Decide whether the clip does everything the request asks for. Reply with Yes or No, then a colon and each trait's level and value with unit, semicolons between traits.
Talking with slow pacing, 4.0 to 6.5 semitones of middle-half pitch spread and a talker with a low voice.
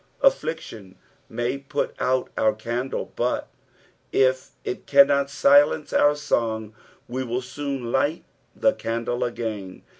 No: slow, 120 wpm; average, 3.2 semitones; low, 130 Hz